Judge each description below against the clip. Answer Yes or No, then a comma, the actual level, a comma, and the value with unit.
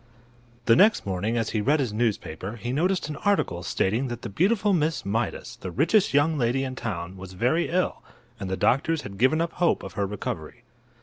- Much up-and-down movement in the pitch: Yes, wide, 8.1 semitones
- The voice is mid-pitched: No, low, 120 Hz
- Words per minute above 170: Yes, average, 200 wpm